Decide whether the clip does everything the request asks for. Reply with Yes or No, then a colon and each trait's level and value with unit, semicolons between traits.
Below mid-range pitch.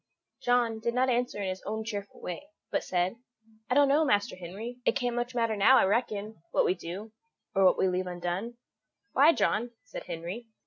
No: high, 220 Hz